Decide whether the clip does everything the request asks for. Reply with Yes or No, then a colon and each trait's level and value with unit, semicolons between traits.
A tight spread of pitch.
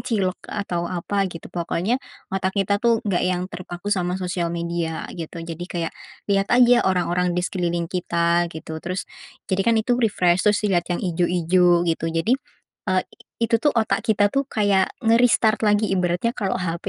No: average, 3.1 semitones